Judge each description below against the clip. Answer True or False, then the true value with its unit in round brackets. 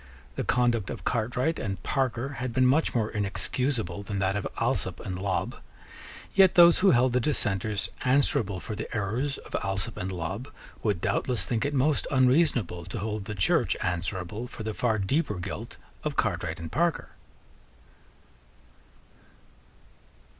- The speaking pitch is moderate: False (110 Hz)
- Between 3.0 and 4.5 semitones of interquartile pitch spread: False (5.0 semitones)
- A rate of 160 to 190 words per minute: False (150 wpm)